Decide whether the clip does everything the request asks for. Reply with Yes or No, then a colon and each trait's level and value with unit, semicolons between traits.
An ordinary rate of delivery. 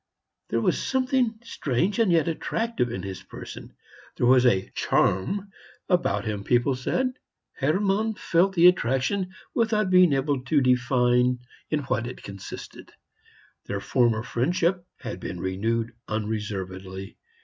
No: slow, 130 wpm